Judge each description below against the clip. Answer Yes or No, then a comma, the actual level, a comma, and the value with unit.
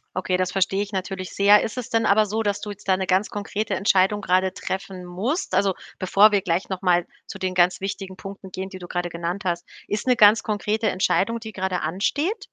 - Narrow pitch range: Yes, narrow, 2.0 semitones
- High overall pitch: Yes, high, 195 Hz